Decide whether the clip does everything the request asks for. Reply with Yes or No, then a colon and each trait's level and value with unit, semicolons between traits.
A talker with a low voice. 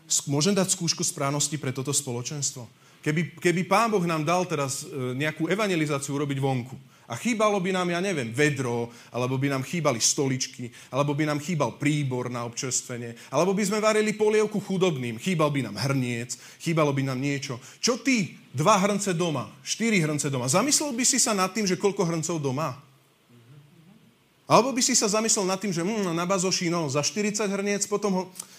No: medium, 155 Hz